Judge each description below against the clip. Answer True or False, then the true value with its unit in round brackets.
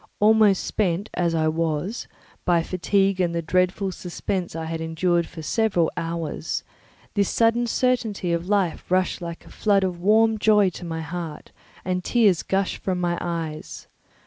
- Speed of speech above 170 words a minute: False (155 wpm)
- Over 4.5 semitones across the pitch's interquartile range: False (3.3 semitones)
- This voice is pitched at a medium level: True (180 Hz)